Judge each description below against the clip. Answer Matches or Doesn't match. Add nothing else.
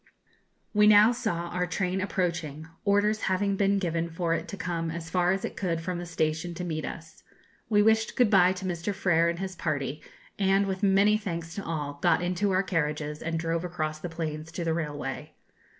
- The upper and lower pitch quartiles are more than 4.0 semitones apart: Doesn't match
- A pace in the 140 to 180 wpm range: Doesn't match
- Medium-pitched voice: Matches